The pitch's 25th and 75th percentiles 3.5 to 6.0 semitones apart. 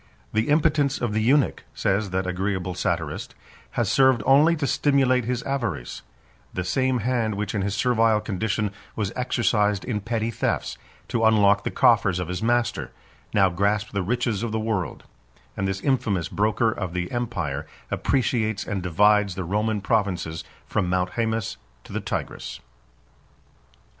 Yes: average, 4.1 semitones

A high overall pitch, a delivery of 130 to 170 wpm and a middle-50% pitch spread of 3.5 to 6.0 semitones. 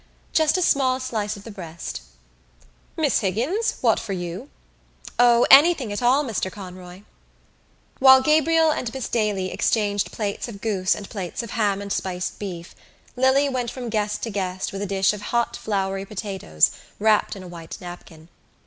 Yes: high, 210 Hz; average, 165 wpm; average, 4.6 semitones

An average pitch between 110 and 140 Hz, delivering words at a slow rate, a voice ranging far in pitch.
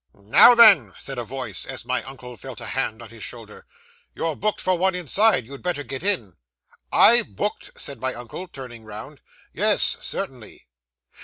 No: low, 135 Hz; average, 170 wpm; wide, 7.6 semitones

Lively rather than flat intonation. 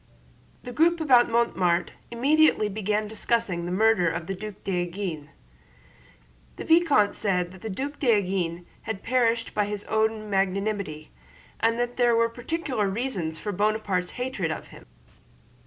No: average, 4.2 semitones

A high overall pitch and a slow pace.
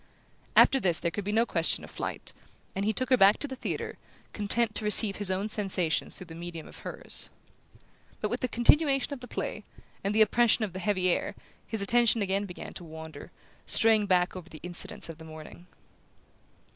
No: high, 200 Hz; average, 200 wpm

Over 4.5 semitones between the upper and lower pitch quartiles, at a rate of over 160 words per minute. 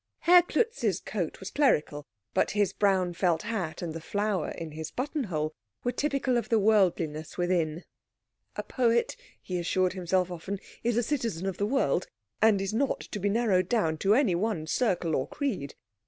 Yes: average, 5.2 semitones; average, 175 wpm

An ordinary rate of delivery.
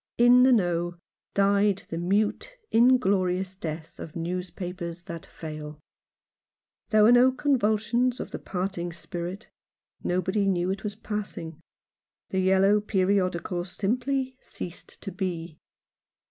No: slow, 120 wpm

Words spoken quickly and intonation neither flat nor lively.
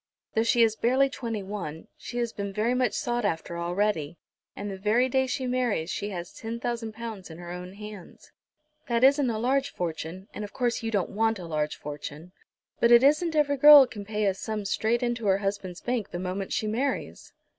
Yes: fast, 210 wpm; average, 4.3 semitones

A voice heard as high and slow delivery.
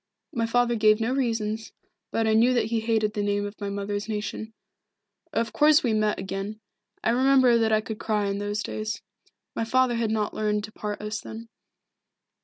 No: high, 220 Hz; average, 195 wpm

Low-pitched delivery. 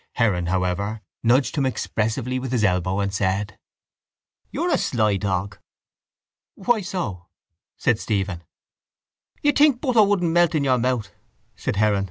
Yes: low, 110 Hz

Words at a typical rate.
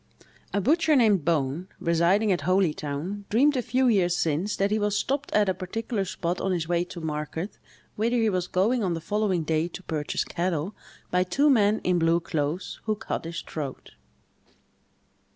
Yes: average, 180 wpm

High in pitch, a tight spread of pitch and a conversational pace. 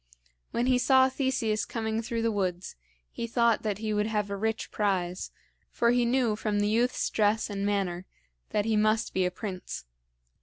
Yes: high, 215 Hz; narrow, 2.3 semitones; average, 185 wpm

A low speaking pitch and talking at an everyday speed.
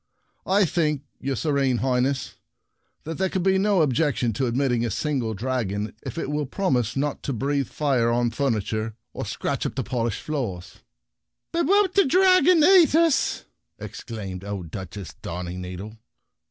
Yes: low, 130 Hz; average, 170 wpm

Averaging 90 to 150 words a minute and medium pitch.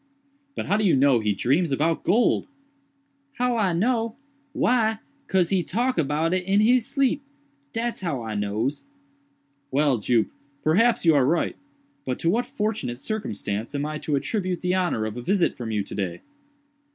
No: average, 170 wpm; medium, 175 Hz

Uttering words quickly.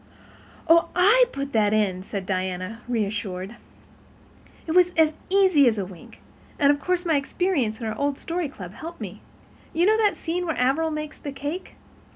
No: average, 170 wpm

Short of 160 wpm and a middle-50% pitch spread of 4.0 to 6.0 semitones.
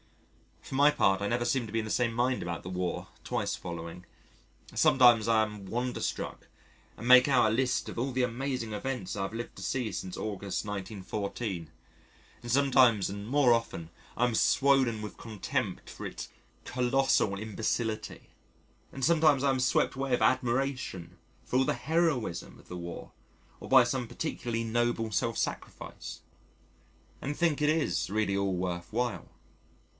No: average, 165 wpm; average, 4.3 semitones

